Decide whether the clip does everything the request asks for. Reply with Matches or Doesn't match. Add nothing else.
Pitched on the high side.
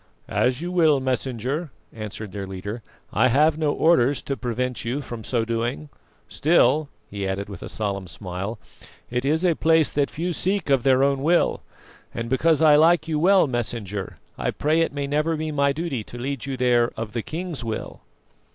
Doesn't match